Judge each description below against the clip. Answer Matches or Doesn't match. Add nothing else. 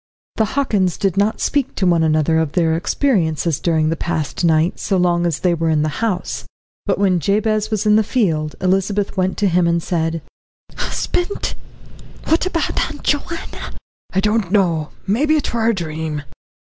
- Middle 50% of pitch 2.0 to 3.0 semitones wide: Doesn't match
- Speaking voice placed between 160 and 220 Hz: Matches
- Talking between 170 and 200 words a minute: Matches